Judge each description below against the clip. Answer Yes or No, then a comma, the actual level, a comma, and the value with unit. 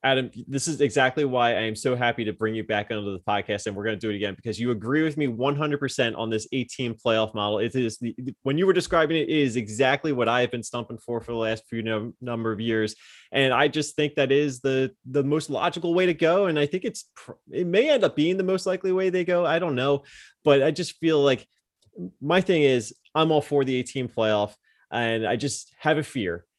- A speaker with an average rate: No, fast, 250 wpm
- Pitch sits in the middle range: No, low, 130 Hz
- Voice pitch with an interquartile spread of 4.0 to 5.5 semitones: Yes, average, 4.7 semitones